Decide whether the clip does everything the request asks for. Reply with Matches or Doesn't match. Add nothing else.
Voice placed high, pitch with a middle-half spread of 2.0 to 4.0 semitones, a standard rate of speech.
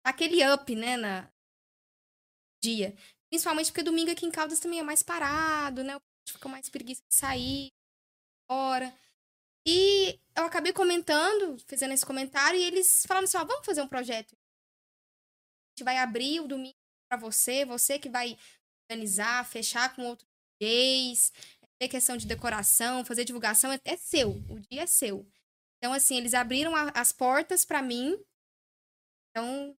Doesn't match